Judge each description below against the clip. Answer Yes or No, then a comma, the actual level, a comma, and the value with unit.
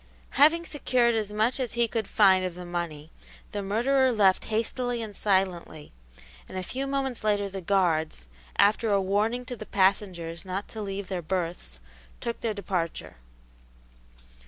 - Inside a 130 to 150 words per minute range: No, average, 160 wpm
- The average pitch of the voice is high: Yes, high, 200 Hz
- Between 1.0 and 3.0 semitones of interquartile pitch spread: No, average, 4.1 semitones